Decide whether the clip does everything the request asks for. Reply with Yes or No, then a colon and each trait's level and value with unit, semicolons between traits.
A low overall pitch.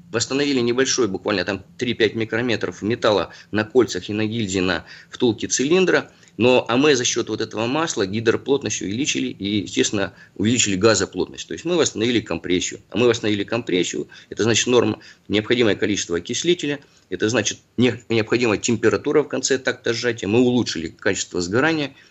Yes: low, 115 Hz